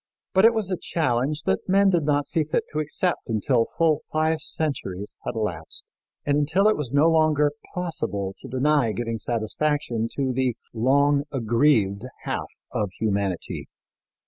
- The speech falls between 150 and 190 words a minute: Yes, average, 155 wpm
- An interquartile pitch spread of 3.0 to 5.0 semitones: No, wide, 5.4 semitones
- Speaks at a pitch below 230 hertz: Yes, medium, 140 Hz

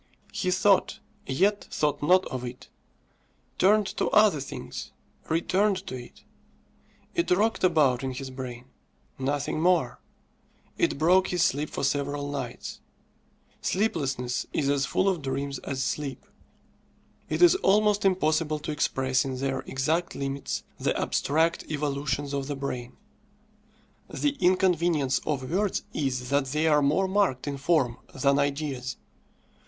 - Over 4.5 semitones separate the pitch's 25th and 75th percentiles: Yes, average, 5.1 semitones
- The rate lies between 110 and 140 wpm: Yes, slow, 135 wpm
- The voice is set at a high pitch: No, medium, 145 Hz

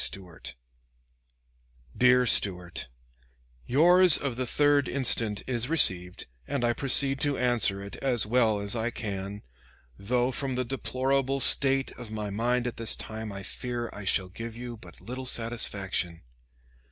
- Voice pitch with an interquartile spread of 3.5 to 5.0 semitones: Yes, average, 4.2 semitones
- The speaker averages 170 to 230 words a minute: No, average, 145 wpm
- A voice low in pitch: Yes, low, 120 Hz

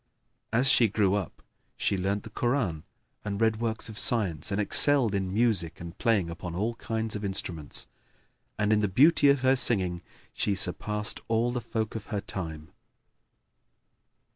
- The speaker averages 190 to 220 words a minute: No, average, 165 wpm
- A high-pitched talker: No, low, 105 Hz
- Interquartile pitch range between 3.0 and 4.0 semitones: Yes, average, 3.5 semitones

